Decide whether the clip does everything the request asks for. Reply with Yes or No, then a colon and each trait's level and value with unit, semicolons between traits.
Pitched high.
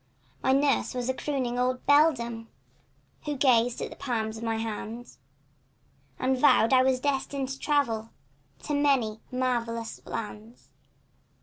Yes: very high, 250 Hz